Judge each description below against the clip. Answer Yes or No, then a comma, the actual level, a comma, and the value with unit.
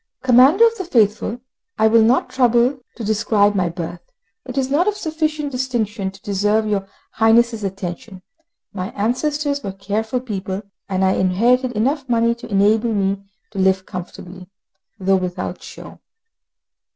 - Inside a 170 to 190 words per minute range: No, average, 150 wpm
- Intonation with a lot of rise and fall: No, average, 4.5 semitones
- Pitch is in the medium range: No, high, 220 Hz